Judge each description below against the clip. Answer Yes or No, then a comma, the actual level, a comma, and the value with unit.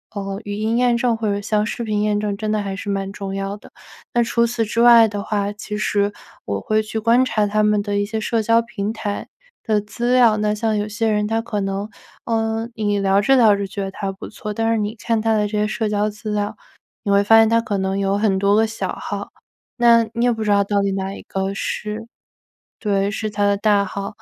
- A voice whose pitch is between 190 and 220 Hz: Yes, high, 210 Hz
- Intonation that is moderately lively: No, narrow, 1.8 semitones